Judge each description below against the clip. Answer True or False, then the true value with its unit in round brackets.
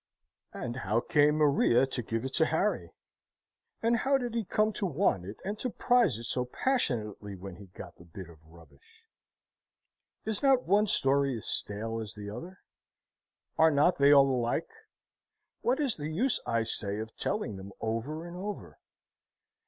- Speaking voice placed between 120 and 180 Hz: True (135 Hz)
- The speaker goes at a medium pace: True (170 wpm)